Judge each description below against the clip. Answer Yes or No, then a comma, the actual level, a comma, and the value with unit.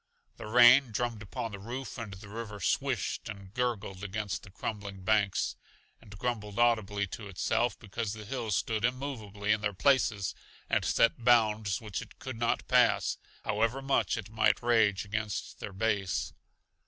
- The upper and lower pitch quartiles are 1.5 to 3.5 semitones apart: Yes, average, 2.7 semitones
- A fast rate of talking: No, average, 160 wpm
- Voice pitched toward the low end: Yes, low, 110 Hz